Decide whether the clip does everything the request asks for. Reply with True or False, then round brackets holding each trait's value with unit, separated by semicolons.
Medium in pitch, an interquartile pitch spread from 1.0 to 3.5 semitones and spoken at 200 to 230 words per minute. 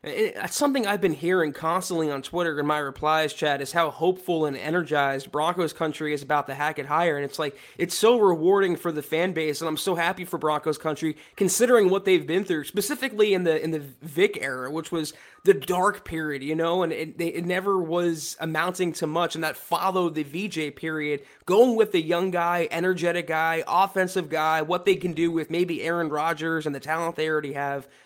True (165 Hz; 2.9 semitones; 205 wpm)